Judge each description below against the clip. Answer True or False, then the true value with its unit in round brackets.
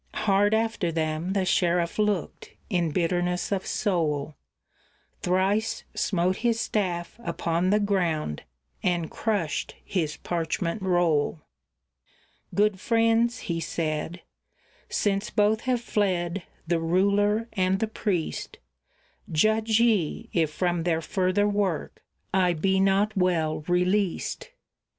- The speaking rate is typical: False (115 wpm)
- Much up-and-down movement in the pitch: False (3.4 semitones)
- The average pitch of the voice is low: False (185 Hz)